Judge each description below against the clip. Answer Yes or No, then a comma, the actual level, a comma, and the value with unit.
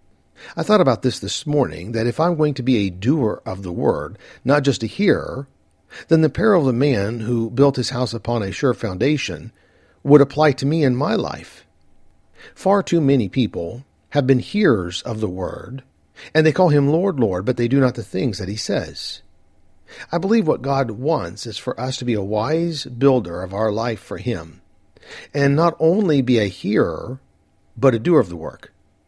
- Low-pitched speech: Yes, low, 125 Hz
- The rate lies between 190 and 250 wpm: Yes, average, 200 wpm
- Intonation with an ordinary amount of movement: No, wide, 5.7 semitones